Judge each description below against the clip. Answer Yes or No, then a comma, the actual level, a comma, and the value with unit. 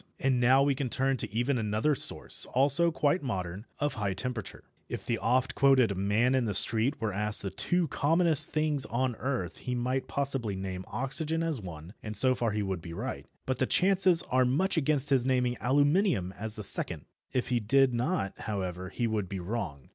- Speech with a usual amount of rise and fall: Yes, average, 5.0 semitones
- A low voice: Yes, low, 125 Hz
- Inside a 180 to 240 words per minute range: Yes, average, 200 wpm